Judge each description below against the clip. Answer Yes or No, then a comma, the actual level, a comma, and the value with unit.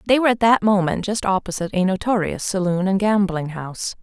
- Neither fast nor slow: Yes, average, 195 wpm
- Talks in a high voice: Yes, high, 195 Hz